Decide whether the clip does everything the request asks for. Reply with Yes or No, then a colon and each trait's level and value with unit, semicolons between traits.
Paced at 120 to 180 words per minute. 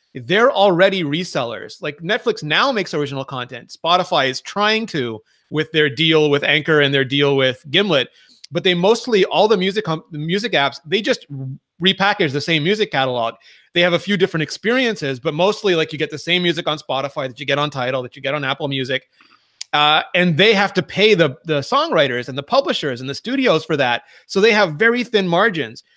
No: fast, 205 wpm